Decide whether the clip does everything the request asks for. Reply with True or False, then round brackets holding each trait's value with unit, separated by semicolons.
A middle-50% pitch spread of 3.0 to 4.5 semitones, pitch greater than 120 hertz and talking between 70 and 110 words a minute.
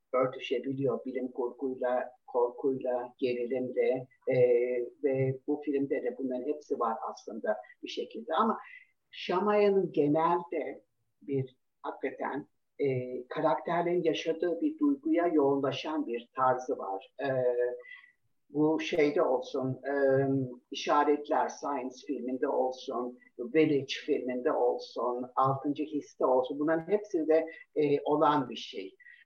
True (4.2 semitones; 140 Hz; 105 wpm)